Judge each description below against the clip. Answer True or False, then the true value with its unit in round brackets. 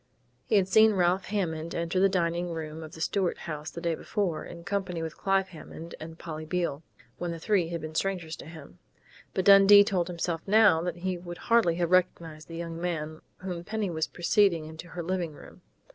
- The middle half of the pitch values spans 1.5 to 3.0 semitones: True (2.6 semitones)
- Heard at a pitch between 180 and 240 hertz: False (170 Hz)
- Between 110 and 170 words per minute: False (205 wpm)